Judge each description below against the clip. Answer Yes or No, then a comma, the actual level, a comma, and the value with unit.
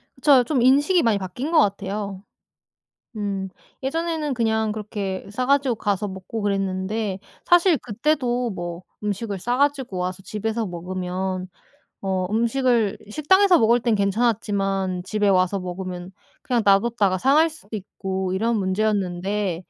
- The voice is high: Yes, high, 210 Hz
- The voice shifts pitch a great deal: No, average, 4.4 semitones